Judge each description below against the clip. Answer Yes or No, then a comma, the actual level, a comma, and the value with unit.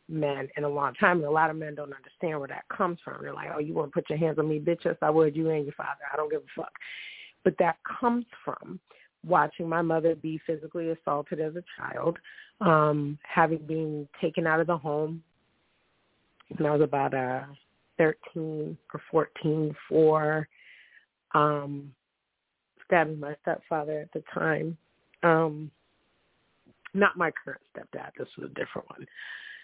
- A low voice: No, medium, 155 Hz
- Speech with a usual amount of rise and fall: No, narrow, 1.7 semitones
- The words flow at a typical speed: Yes, average, 170 wpm